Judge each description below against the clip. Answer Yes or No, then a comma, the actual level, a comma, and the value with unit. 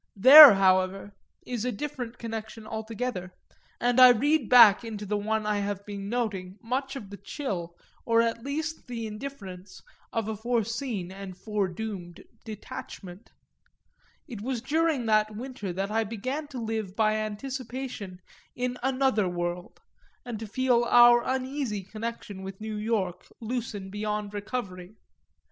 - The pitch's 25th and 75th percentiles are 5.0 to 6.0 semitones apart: No, average, 3.6 semitones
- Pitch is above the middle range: Yes, high, 220 Hz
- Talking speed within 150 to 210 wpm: No, average, 140 wpm